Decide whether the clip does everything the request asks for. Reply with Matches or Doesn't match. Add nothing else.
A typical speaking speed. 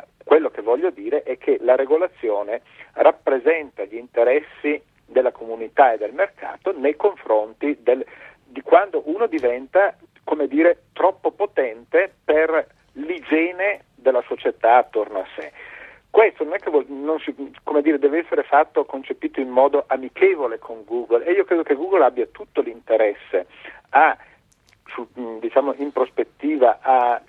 Matches